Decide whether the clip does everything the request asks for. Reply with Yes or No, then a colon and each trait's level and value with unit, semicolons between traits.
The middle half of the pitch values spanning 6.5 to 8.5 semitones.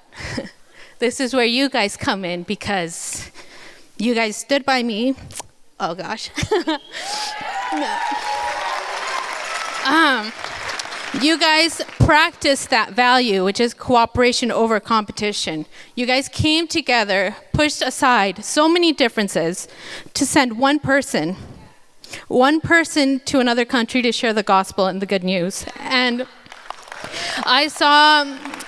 No: average, 5.2 semitones